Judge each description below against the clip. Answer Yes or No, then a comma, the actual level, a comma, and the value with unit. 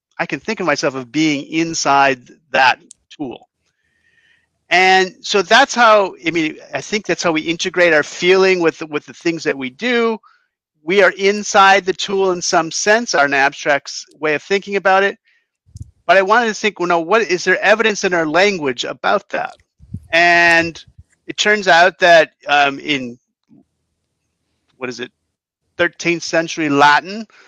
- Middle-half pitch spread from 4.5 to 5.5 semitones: Yes, average, 5.1 semitones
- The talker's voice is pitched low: No, medium, 180 Hz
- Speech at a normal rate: Yes, average, 170 wpm